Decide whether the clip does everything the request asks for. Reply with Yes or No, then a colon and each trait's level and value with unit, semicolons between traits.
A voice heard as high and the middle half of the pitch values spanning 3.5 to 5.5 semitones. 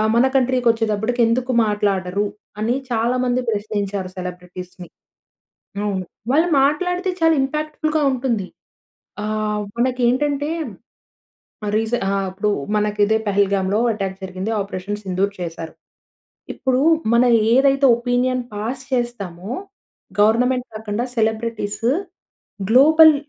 Yes: high, 225 Hz; average, 4.0 semitones